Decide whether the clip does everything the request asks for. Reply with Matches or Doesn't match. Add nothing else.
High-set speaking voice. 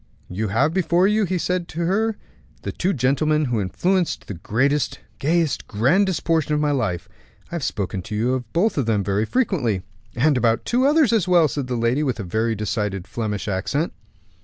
Doesn't match